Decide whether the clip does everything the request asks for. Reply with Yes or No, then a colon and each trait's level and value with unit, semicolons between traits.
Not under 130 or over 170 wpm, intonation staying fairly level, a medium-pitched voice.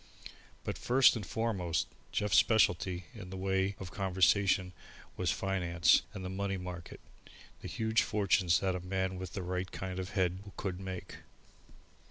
No: average, 155 wpm; narrow, 1.4 semitones; very low, 95 Hz